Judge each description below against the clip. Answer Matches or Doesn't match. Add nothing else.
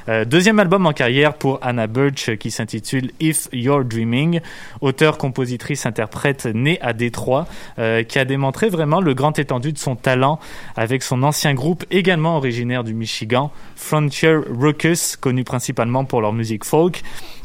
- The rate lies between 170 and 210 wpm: Doesn't match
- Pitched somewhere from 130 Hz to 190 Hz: Matches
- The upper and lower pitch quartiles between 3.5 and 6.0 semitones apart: Matches